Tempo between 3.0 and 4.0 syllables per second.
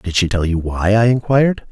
No: 5.4 syllables/s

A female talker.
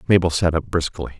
No: male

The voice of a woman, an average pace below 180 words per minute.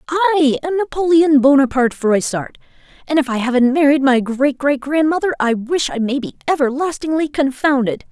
Yes: female; average, 155 wpm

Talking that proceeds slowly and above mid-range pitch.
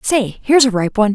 No: fast, 210 wpm; high, 230 Hz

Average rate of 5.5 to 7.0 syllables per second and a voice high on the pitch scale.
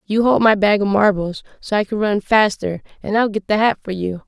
No: 5.3 syllables/s; high, 205 Hz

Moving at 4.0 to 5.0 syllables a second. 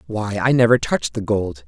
No: 5.4 syllables/s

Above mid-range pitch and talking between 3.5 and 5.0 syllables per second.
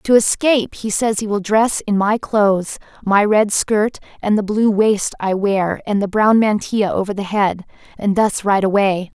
Yes: high, 205 Hz; 4.5 syllables/s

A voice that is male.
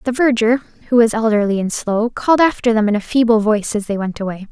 No: female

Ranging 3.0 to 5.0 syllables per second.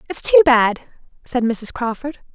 Yes: 4.5 syllables/s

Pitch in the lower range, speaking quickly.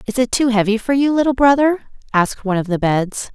No: high, 235 Hz; fast, 235 wpm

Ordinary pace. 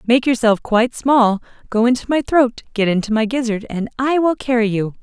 Yes: average, 190 wpm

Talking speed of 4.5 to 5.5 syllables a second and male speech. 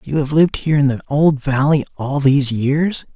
Yes: 5.4 syllables/s; male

